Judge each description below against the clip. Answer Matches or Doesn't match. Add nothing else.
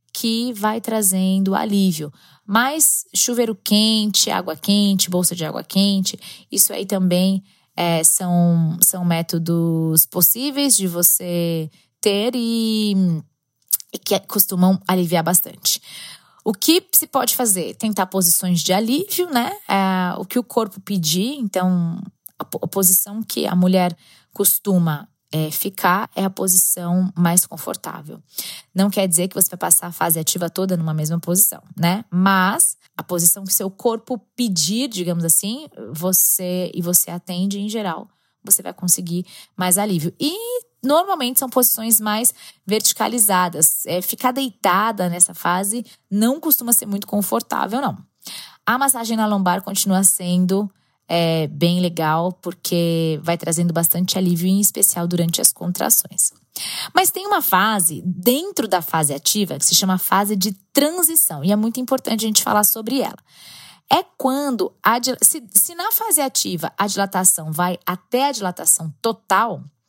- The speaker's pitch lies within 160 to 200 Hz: Matches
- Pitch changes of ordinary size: Matches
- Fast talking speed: Doesn't match